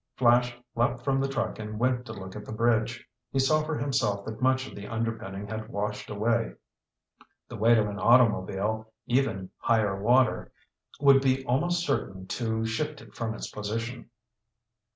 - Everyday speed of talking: Yes, average, 170 wpm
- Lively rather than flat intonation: No, average, 3.3 semitones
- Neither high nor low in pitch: No, low, 115 Hz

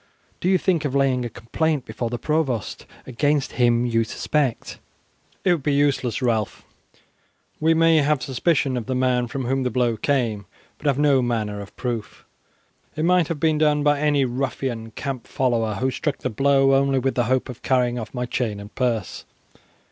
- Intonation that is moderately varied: Yes, average, 3.4 semitones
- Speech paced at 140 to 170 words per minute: No, average, 185 wpm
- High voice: No, low, 130 Hz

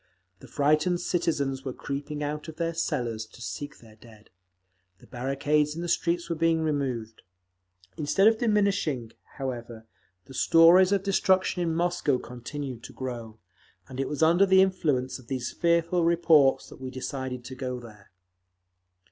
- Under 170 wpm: Yes, average, 155 wpm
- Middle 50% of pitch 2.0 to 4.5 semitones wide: No, average, 4.9 semitones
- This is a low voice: No, medium, 145 Hz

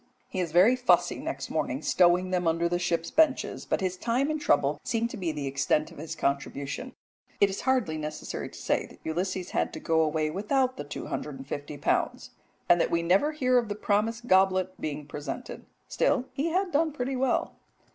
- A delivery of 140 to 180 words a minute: No, average, 195 wpm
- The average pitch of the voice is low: No, medium, 185 Hz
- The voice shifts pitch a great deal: Yes, wide, 8.1 semitones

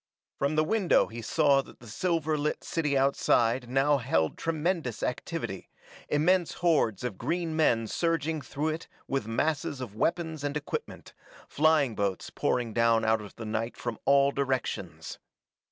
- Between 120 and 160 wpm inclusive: Yes, average, 155 wpm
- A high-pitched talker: No, medium, 140 Hz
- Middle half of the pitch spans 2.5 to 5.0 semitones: No, wide, 5.5 semitones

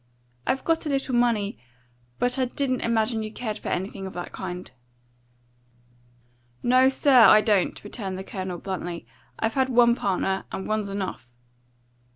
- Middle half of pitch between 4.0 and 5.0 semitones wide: Yes, average, 4.6 semitones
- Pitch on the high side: Yes, high, 215 Hz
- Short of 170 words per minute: Yes, average, 155 wpm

